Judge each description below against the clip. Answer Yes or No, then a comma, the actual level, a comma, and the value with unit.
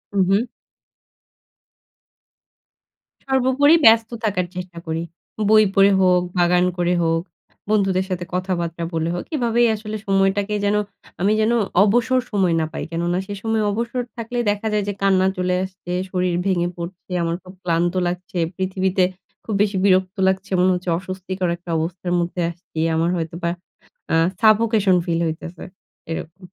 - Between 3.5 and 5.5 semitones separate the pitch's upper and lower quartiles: No, average, 2.9 semitones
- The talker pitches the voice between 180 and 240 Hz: Yes, medium, 185 Hz